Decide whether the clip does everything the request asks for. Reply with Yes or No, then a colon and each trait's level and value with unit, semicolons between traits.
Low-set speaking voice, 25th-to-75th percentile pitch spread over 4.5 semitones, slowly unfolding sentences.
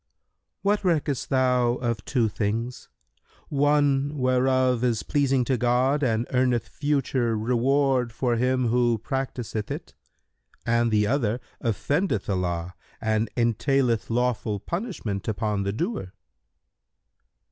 No: low, 125 Hz; average, 3.2 semitones; slow, 115 wpm